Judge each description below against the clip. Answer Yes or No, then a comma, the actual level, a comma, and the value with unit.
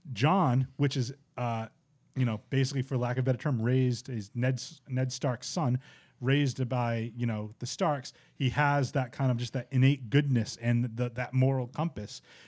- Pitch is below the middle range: Yes, low, 130 Hz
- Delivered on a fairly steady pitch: Yes, narrow, 2.2 semitones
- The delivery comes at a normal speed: Yes, average, 190 wpm